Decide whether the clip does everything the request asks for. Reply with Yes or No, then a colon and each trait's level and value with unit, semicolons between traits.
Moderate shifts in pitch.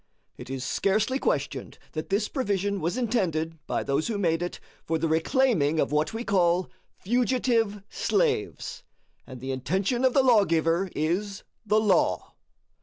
No: wide, 6.2 semitones